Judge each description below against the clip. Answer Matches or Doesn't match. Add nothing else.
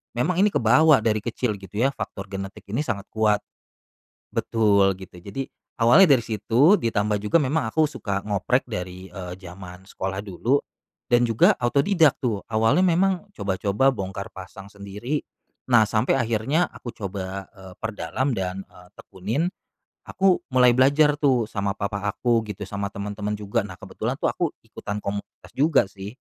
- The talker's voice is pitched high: Doesn't match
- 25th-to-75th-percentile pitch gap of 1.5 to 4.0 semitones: Doesn't match